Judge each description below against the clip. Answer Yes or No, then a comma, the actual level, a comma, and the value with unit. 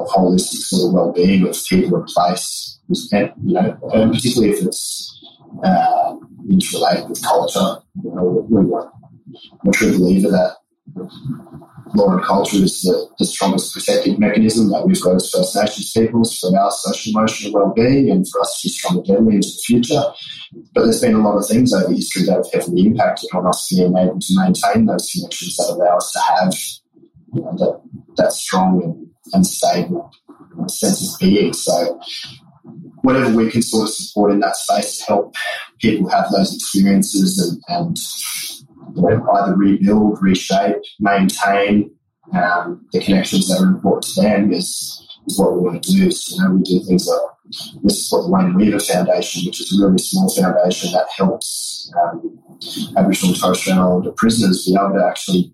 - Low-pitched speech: Yes, low, 105 Hz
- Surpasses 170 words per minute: Yes, average, 185 wpm